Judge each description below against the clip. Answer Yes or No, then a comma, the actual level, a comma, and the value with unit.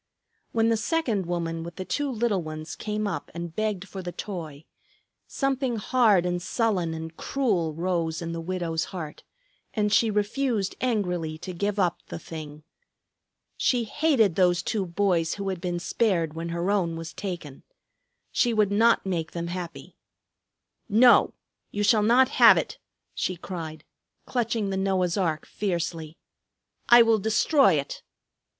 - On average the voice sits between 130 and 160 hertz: No, medium, 185 Hz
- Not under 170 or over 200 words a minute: No, average, 155 wpm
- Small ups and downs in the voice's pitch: No, average, 4.5 semitones